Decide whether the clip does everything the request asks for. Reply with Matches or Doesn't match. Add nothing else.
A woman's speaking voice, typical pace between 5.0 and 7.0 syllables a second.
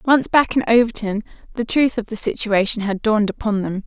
Matches